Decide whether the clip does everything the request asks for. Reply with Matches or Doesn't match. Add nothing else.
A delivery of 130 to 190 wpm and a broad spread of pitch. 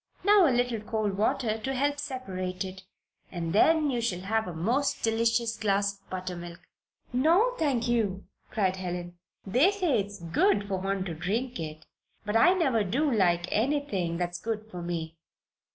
Matches